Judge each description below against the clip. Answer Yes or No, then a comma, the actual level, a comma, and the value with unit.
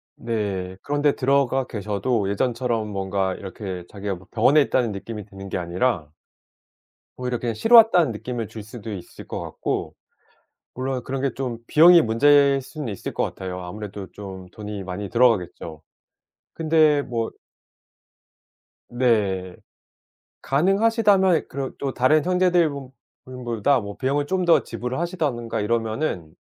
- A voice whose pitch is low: Yes, low, 120 Hz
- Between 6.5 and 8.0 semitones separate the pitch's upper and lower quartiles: No, wide, 5.7 semitones